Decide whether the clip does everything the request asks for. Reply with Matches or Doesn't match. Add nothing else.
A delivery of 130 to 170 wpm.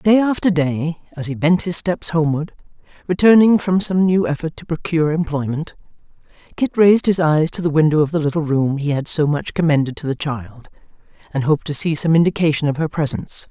Doesn't match